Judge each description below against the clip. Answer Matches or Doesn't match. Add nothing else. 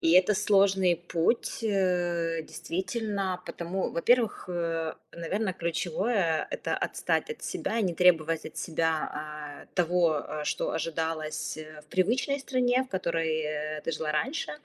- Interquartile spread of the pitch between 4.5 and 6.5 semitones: Doesn't match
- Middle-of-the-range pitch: Matches